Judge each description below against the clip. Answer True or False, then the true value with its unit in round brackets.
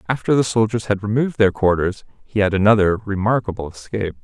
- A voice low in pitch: True (105 Hz)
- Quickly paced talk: False (170 wpm)